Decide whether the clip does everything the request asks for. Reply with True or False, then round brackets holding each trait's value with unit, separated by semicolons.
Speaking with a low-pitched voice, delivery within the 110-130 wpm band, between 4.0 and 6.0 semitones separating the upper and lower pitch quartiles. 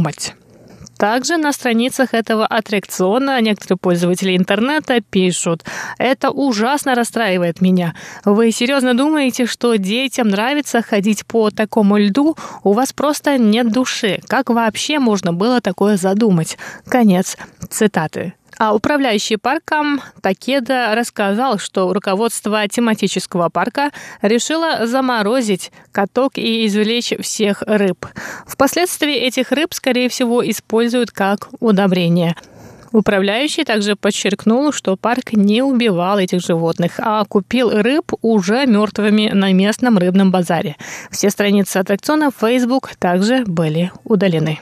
False (220 Hz; 115 wpm; 4.3 semitones)